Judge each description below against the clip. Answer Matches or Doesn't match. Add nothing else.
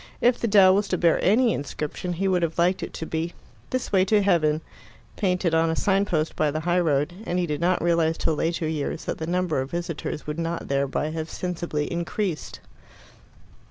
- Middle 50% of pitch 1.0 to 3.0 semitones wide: Matches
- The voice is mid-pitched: Matches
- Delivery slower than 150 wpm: Doesn't match